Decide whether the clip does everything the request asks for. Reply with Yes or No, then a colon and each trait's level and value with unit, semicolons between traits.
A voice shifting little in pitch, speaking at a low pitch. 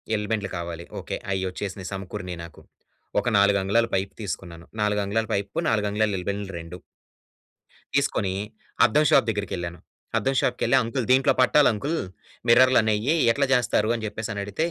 No: average, 3.3 semitones; low, 105 Hz